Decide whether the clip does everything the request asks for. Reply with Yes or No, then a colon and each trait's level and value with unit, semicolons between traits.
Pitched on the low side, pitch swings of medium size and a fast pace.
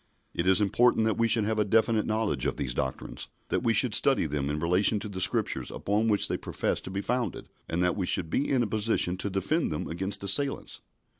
Yes: low, 105 Hz; average, 3.9 semitones; fast, 230 wpm